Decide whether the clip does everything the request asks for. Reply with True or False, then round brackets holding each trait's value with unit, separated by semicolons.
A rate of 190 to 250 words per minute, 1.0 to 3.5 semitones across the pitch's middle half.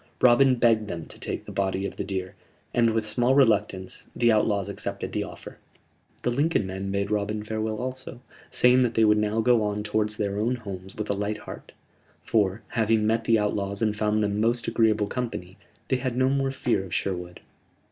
True (200 wpm; 2.8 semitones)